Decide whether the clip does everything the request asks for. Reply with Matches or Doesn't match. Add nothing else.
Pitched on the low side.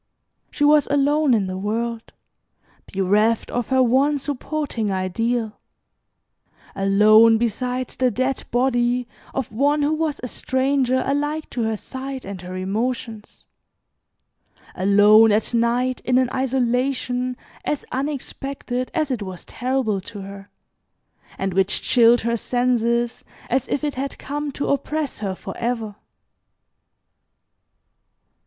Doesn't match